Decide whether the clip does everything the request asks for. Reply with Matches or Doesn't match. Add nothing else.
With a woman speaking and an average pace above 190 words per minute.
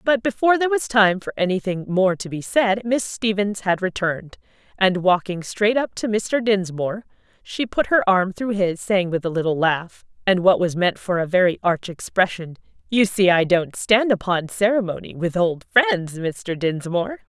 Doesn't match